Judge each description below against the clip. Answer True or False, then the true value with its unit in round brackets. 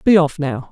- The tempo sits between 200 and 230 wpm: False (250 wpm)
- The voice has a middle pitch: True (155 Hz)